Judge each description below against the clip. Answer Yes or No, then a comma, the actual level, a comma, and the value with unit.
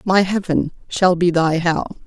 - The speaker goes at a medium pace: Yes, average, 175 wpm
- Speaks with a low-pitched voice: No, medium, 175 Hz